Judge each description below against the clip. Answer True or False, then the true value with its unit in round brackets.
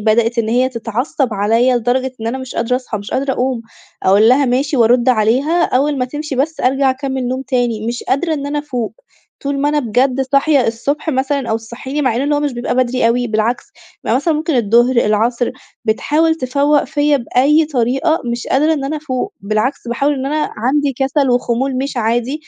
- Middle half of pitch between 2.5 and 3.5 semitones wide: True (3.1 semitones)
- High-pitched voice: True (255 Hz)